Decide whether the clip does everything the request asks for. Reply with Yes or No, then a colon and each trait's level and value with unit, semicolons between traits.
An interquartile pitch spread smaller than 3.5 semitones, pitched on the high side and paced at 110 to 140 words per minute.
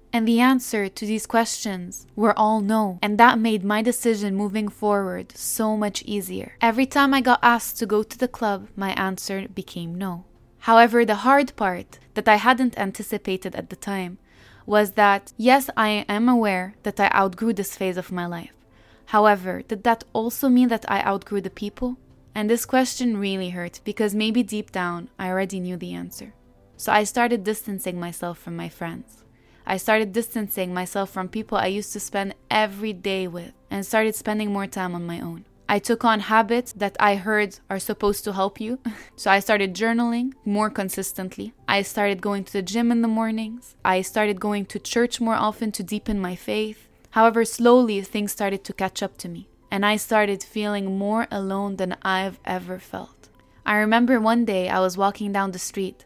No: narrow, 2.6 semitones; high, 210 Hz; average, 190 wpm